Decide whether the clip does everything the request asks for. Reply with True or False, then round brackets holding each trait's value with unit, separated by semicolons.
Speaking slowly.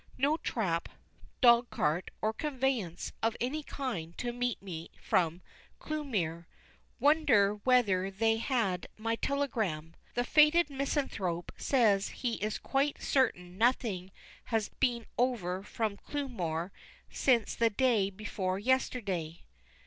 True (120 wpm)